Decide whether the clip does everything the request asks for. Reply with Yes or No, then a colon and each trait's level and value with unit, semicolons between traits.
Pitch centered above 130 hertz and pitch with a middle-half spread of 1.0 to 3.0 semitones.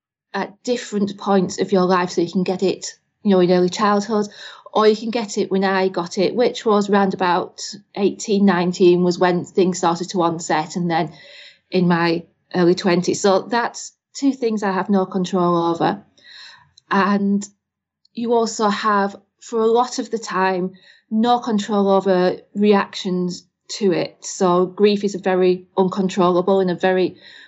Yes: high, 190 Hz; narrow, 2.4 semitones